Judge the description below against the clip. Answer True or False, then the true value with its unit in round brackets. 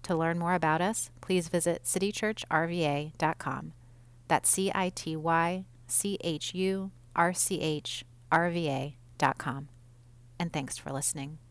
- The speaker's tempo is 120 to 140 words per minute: True (135 wpm)